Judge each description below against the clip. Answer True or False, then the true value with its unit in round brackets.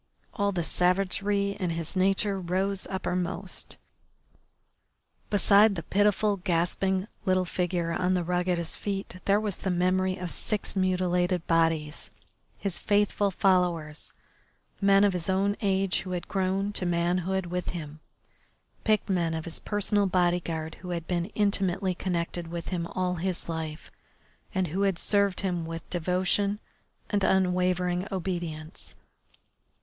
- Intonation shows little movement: True (2.2 semitones)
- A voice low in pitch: False (185 Hz)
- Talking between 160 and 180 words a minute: False (140 wpm)